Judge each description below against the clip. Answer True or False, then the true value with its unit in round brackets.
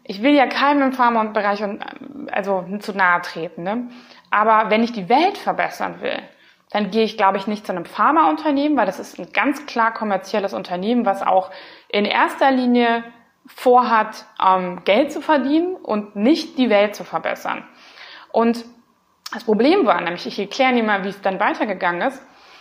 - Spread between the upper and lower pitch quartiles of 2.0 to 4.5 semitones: False (5.0 semitones)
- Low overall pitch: False (220 Hz)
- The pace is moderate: True (175 wpm)